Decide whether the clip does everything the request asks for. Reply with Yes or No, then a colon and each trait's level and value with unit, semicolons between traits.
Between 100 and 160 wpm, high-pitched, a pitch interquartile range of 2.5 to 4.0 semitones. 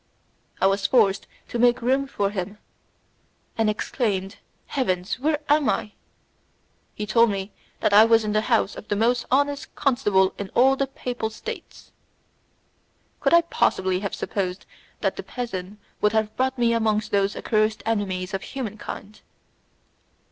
Yes: average, 150 wpm; high, 215 Hz; average, 3.7 semitones